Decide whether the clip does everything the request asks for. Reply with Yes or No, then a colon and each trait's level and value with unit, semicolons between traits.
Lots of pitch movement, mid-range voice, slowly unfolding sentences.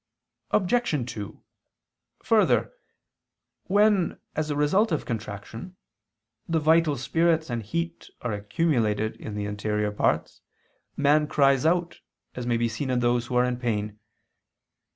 No: wide, 6.8 semitones; low, 130 Hz; slow, 130 wpm